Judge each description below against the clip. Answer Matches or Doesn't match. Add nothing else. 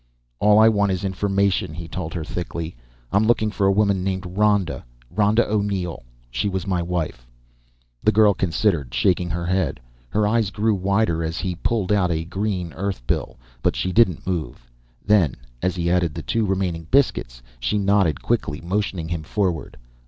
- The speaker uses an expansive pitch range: Doesn't match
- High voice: Doesn't match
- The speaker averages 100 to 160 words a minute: Doesn't match